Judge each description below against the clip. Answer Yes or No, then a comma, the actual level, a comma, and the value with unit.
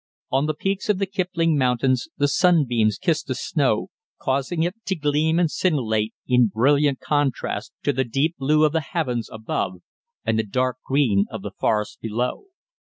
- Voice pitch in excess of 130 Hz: Yes, medium, 140 Hz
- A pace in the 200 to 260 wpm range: No, average, 170 wpm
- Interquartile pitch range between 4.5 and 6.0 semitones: Yes, average, 5.0 semitones